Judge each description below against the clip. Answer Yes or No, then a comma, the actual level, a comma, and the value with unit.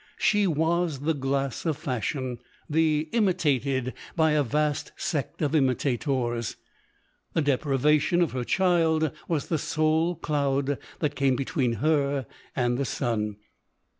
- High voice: No, medium, 145 Hz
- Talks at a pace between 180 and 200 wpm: No, slow, 135 wpm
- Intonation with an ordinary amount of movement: Yes, average, 3.3 semitones